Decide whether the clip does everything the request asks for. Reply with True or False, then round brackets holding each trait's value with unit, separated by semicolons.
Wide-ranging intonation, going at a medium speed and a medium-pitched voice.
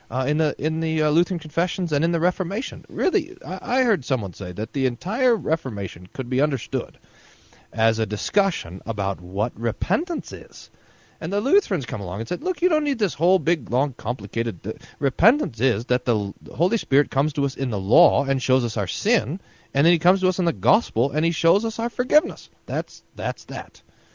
False (7.8 semitones; 210 wpm; 145 Hz)